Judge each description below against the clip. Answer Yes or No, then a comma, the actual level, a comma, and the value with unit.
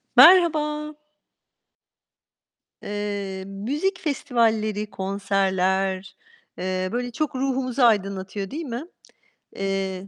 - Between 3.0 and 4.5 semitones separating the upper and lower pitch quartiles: No, wide, 5.5 semitones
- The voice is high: Yes, high, 210 Hz